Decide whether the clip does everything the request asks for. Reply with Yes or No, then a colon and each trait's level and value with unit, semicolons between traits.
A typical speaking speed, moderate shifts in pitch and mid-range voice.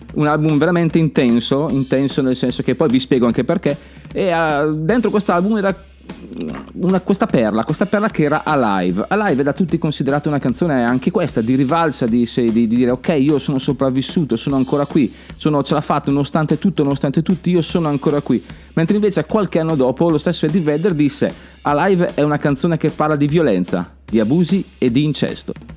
No: fast, 195 wpm; average, 4.4 semitones; medium, 150 Hz